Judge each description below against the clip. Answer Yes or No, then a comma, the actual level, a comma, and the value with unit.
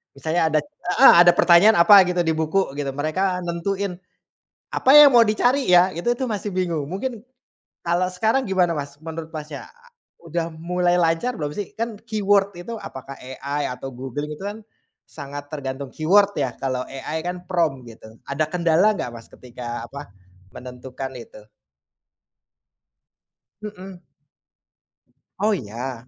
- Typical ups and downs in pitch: No, wide, 5.7 semitones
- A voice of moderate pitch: Yes, medium, 170 Hz